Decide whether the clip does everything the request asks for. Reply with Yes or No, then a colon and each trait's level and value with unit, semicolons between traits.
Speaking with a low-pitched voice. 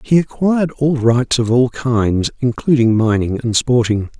Yes: low, 125 Hz